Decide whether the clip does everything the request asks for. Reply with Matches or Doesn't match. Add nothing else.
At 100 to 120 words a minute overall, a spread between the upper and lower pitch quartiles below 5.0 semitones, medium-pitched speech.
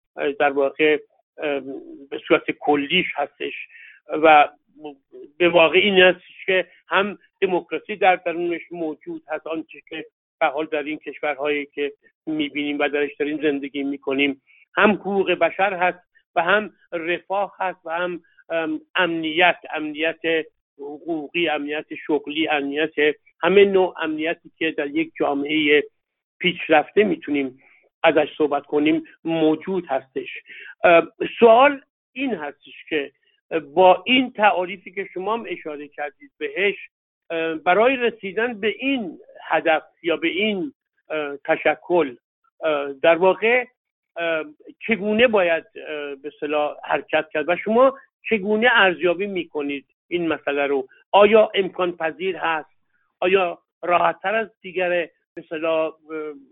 Matches